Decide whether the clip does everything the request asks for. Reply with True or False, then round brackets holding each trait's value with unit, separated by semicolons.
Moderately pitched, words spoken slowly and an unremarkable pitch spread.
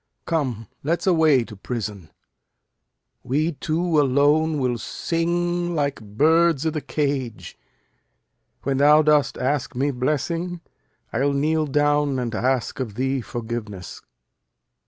True (145 Hz; 115 wpm; 4.0 semitones)